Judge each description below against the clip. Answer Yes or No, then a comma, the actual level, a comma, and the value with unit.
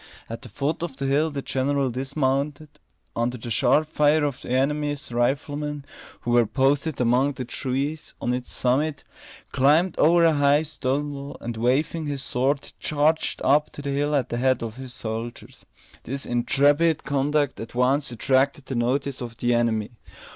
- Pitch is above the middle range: No, medium, 140 Hz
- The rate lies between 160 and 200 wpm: Yes, average, 170 wpm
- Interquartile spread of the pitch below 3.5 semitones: Yes, average, 2.8 semitones